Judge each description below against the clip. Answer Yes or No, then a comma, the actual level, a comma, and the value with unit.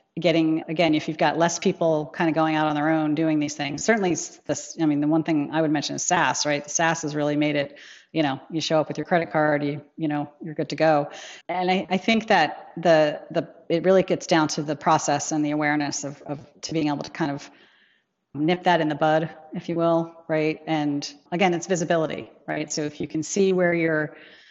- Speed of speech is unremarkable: No, fast, 240 wpm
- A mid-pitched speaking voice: Yes, medium, 155 Hz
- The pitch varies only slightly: Yes, narrow, 2.2 semitones